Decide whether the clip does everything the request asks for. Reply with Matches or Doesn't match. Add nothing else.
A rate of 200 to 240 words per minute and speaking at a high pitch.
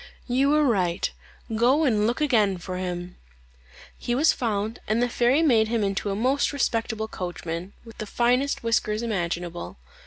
Doesn't match